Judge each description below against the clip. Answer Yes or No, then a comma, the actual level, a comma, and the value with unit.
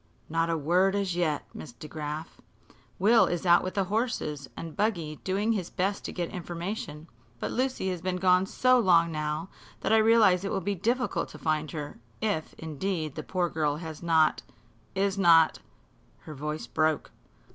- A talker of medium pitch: Yes, medium, 175 Hz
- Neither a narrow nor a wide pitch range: Yes, average, 3.9 semitones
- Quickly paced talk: No, average, 180 wpm